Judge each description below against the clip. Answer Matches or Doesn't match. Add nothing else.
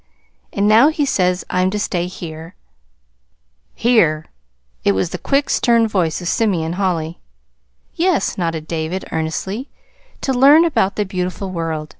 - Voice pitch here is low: Doesn't match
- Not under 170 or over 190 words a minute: Doesn't match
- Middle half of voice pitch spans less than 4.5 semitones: Doesn't match